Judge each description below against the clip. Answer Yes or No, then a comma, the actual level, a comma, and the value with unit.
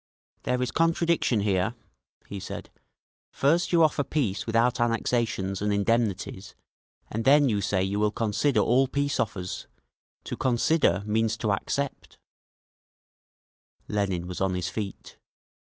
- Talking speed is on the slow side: Yes, slow, 130 wpm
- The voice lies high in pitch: No, low, 110 Hz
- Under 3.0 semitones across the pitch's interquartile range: No, average, 4.9 semitones